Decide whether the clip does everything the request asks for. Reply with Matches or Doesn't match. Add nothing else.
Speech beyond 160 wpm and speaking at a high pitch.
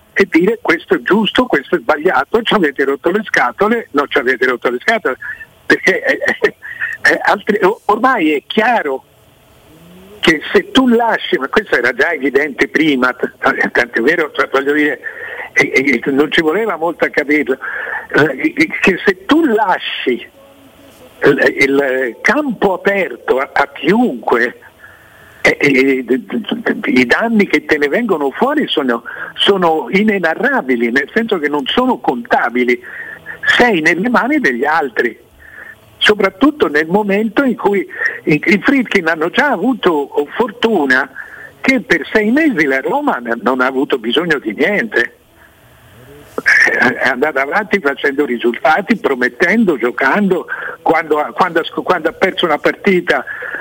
Doesn't match